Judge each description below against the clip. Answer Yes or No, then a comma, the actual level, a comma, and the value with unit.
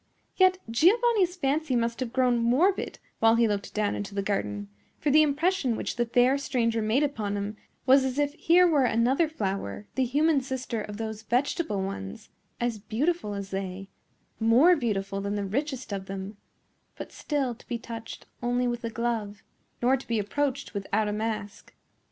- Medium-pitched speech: No, high, 235 Hz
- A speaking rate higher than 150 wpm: Yes, average, 175 wpm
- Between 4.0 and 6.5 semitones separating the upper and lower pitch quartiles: Yes, average, 5.1 semitones